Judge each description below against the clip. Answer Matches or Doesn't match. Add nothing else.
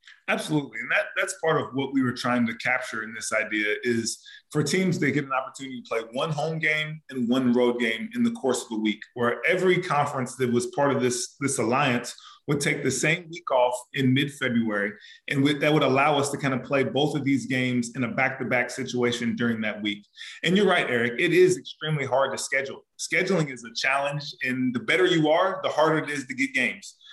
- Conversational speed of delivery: Doesn't match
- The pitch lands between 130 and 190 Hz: Matches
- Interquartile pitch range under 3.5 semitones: Doesn't match